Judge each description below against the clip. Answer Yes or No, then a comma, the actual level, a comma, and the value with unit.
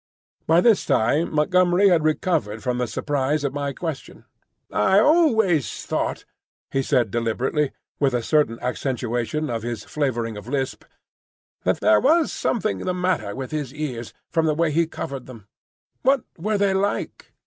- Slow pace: No, average, 160 wpm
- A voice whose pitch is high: No, medium, 145 Hz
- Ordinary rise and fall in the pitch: No, wide, 6.2 semitones